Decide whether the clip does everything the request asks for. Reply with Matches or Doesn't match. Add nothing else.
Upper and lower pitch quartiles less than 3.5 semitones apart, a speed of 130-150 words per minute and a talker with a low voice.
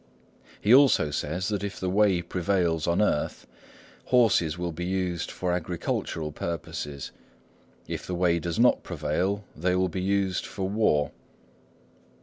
Matches